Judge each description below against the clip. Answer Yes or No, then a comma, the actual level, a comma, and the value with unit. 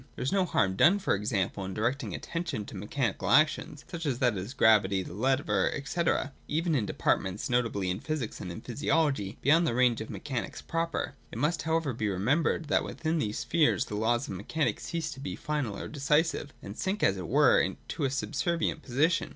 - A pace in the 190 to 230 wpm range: Yes, average, 200 wpm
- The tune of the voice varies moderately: No, wide, 7.1 semitones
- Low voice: Yes, low, 130 Hz